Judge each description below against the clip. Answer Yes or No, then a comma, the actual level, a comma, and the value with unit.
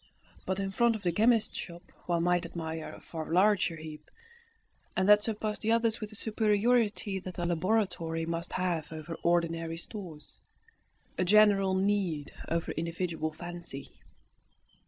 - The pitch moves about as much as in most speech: Yes, average, 3.9 semitones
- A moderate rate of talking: Yes, average, 145 wpm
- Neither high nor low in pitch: Yes, medium, 180 Hz